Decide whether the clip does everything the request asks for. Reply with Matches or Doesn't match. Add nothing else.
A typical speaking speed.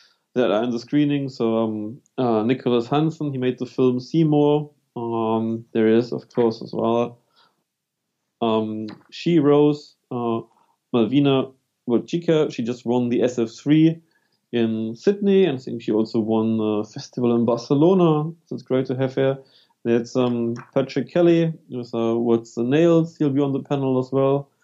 Matches